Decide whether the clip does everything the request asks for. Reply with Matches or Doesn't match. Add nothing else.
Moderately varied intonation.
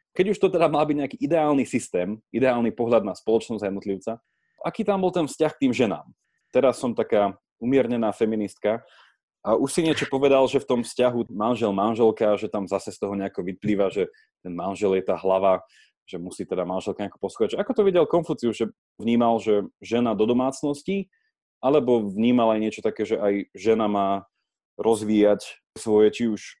Doesn't match